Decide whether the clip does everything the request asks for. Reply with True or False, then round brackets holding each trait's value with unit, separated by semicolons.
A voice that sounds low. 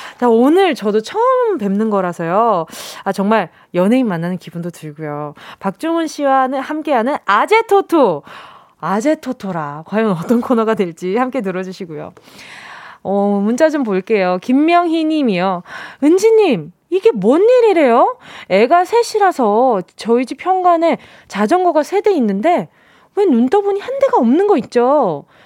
False (255 Hz)